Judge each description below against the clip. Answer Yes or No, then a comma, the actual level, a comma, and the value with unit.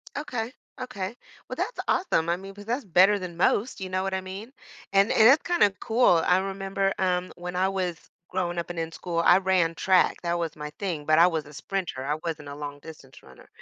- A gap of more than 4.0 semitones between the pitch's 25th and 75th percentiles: No, average, 2.8 semitones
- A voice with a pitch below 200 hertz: Yes, medium, 185 Hz